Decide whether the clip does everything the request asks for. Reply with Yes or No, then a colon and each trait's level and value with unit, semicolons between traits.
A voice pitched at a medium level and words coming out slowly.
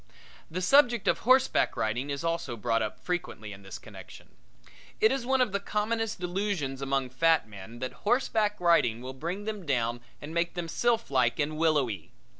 No: medium, 165 Hz; average, 175 wpm